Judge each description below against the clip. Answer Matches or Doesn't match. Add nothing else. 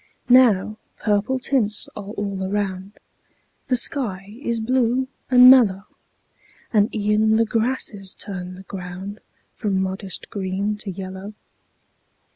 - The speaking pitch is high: Matches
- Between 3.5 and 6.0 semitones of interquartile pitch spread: Doesn't match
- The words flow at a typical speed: Doesn't match